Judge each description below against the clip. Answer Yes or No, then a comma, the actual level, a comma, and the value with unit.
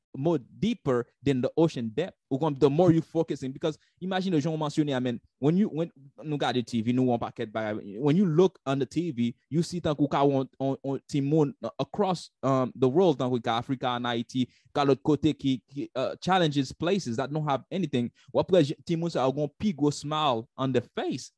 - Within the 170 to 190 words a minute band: Yes, average, 180 wpm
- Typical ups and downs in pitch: Yes, average, 4.0 semitones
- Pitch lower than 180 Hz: Yes, medium, 140 Hz